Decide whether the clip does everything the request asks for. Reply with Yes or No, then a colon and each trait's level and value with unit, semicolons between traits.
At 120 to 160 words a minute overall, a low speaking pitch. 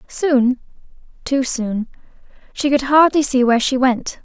No: average, 140 wpm; very high, 260 Hz